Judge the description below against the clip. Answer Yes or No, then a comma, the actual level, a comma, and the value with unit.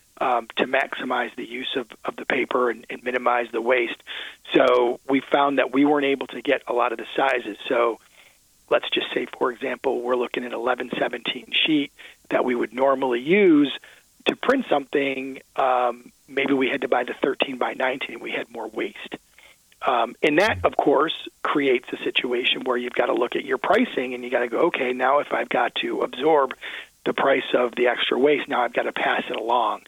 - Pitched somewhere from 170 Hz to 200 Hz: No, low, 135 Hz